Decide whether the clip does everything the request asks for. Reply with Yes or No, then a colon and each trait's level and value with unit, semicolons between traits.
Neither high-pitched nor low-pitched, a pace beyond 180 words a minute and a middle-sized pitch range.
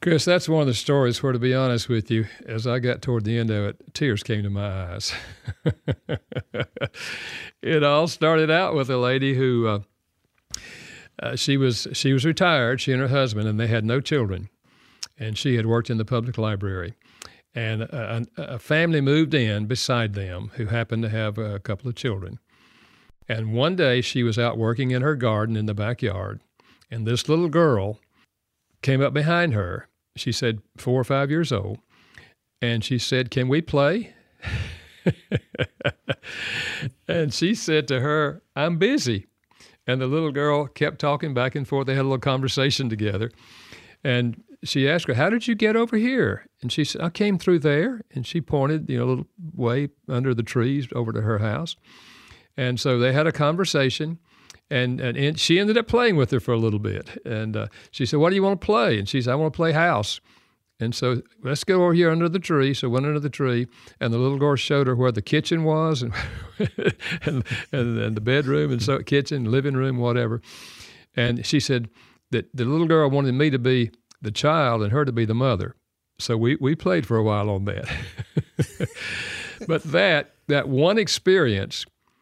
No: low, 130 Hz; average, 195 wpm; average, 4.7 semitones